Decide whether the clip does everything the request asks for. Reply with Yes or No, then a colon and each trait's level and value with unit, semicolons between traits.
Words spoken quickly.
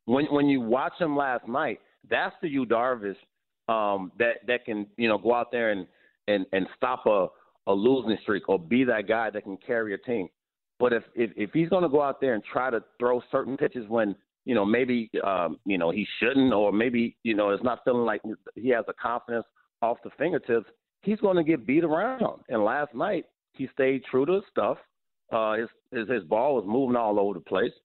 Yes: fast, 220 wpm